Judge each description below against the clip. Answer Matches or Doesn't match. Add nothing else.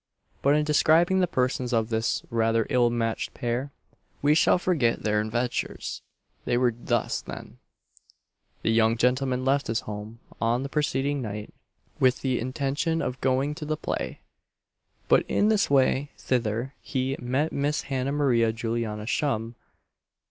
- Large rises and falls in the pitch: Doesn't match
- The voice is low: Matches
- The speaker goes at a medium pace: Matches